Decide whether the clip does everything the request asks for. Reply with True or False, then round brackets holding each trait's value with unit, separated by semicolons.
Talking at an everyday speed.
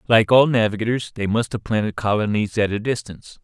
True (190 wpm)